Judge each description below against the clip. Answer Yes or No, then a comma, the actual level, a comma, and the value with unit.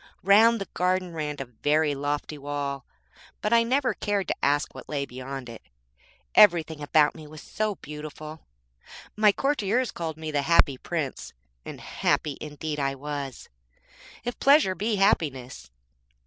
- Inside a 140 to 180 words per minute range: Yes, average, 150 wpm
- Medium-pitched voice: Yes, medium, 155 Hz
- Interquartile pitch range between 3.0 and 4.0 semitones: No, wide, 5.6 semitones